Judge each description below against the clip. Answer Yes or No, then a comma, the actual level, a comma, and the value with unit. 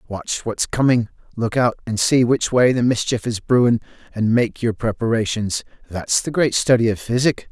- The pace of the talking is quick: No, average, 185 wpm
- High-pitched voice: No, low, 115 Hz